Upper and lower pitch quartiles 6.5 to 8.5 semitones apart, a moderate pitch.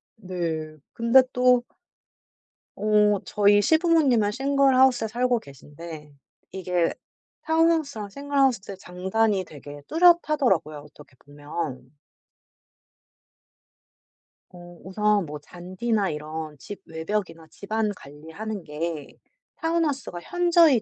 No: wide, 7.6 semitones; high, 205 Hz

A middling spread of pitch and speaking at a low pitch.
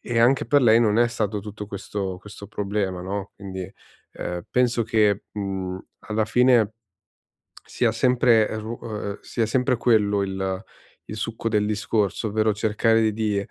No: narrow, 2.2 semitones; low, 105 Hz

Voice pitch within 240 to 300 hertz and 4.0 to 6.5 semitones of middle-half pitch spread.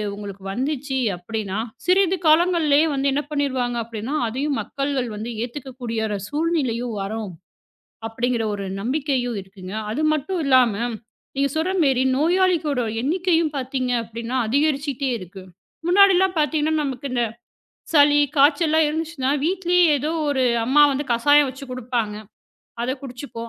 Yes: very high, 270 Hz; average, 4.5 semitones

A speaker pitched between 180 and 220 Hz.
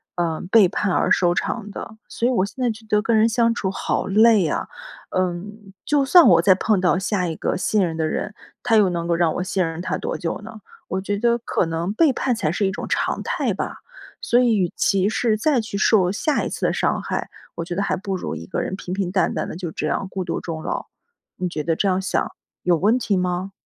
Yes: high, 195 Hz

